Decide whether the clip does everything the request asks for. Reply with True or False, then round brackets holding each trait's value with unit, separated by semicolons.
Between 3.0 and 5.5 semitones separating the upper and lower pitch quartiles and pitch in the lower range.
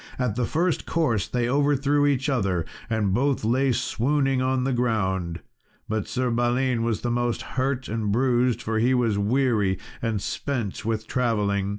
True (3.3 semitones; 120 Hz)